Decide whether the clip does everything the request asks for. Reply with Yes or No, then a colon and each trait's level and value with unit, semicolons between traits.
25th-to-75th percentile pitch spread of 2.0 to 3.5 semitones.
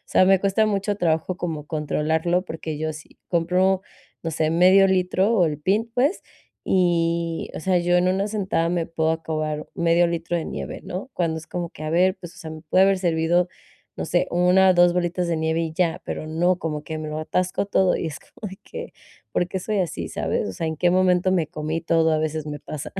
Yes: narrow, 2.6 semitones